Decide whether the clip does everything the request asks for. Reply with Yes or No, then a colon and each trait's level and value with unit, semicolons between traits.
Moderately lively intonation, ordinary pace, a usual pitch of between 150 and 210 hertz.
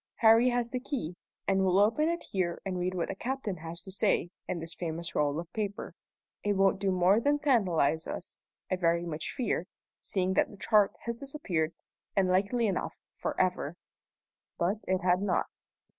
Yes: average, 4.3 semitones; average, 185 wpm; high, 190 Hz